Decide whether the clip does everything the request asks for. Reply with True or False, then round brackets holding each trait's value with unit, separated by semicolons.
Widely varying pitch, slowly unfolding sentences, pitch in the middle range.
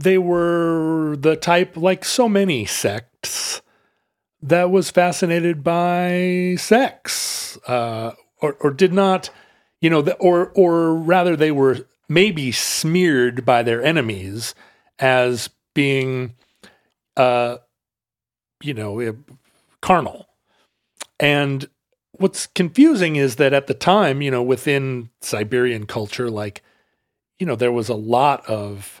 True (6.3 semitones; 120 wpm; 145 Hz)